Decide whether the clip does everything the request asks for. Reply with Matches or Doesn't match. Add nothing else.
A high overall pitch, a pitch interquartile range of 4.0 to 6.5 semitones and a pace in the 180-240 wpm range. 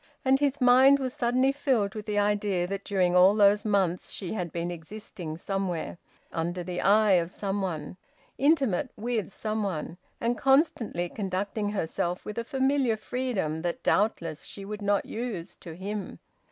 Doesn't match